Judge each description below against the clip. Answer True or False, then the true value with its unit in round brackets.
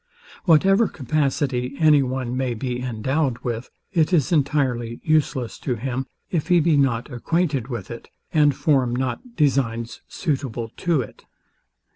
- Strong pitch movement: False (4.0 semitones)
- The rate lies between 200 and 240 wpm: False (140 wpm)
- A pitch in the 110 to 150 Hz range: True (135 Hz)